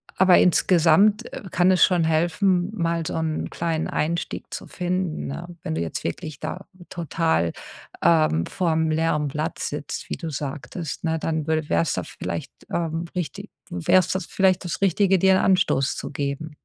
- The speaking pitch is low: No, medium, 165 Hz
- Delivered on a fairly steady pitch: No, average, 3.0 semitones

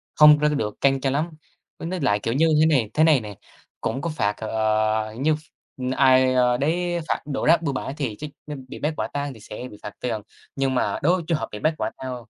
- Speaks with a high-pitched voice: No, low, 135 Hz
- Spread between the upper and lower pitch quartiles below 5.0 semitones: No, wide, 5.4 semitones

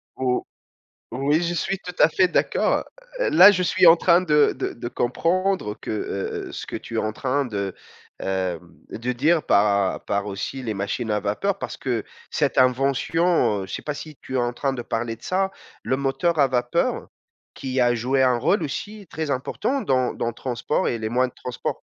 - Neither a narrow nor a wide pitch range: No, wide, 6.2 semitones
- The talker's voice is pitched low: Yes, low, 130 Hz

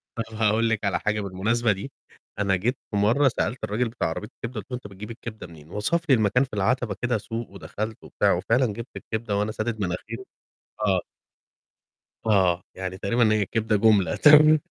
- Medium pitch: No, low, 110 Hz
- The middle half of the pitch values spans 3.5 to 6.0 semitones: No, average, 2.9 semitones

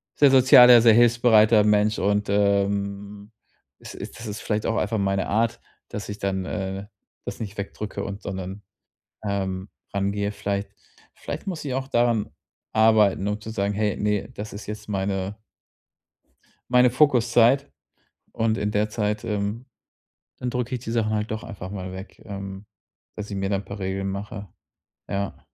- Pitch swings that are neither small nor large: No, narrow, 2.2 semitones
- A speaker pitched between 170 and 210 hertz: No, low, 105 Hz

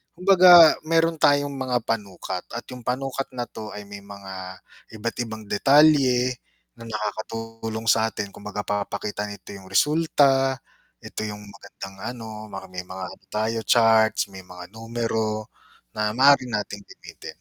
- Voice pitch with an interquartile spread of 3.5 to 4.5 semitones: Yes, average, 4.0 semitones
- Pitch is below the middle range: Yes, low, 110 Hz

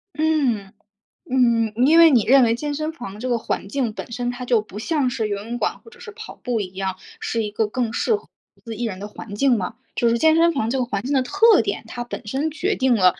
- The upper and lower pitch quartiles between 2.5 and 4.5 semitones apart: No, average, 5.1 semitones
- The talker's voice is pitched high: Yes, high, 245 Hz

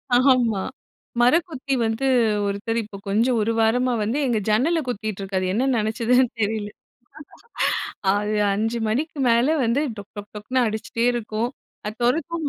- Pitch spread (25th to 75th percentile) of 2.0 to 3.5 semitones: Yes, average, 3.2 semitones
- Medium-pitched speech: No, high, 230 Hz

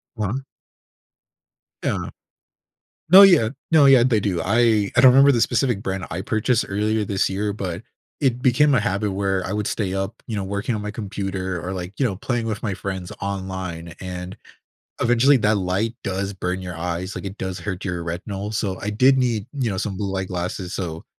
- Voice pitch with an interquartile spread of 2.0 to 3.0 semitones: No, average, 3.4 semitones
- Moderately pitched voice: No, low, 100 Hz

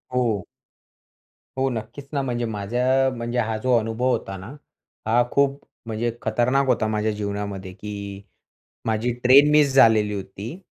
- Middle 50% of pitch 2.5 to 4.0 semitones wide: Yes, average, 3.4 semitones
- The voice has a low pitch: Yes, low, 115 Hz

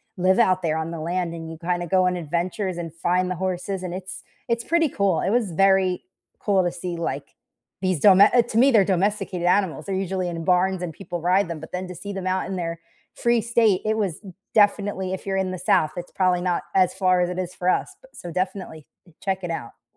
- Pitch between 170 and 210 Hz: Yes, medium, 185 Hz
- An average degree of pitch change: No, narrow, 1.9 semitones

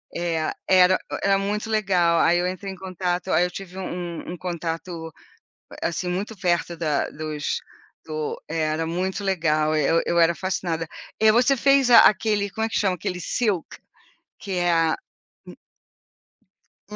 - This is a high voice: No, medium, 180 Hz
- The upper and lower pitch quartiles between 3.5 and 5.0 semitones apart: No, average, 2.9 semitones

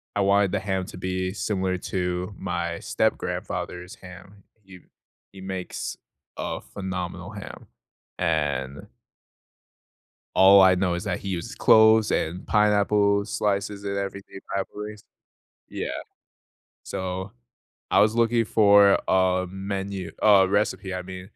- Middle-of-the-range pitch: No, very low, 95 Hz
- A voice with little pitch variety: Yes, narrow, 1.7 semitones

